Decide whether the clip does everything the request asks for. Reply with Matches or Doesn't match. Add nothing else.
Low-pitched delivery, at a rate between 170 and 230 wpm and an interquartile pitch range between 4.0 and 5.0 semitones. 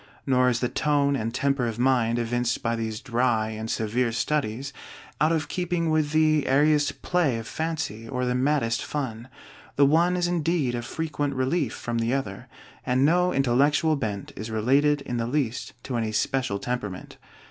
Matches